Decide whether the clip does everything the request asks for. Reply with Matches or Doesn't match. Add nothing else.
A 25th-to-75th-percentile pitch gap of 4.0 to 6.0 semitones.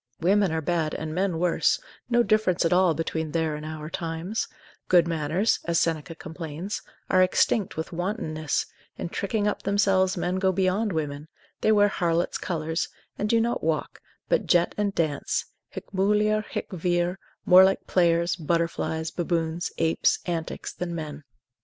Doesn't match